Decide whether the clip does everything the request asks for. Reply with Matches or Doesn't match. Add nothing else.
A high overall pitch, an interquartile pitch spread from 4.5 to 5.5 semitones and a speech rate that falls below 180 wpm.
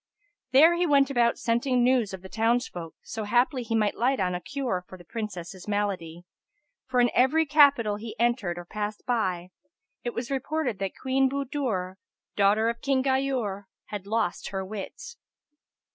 Matches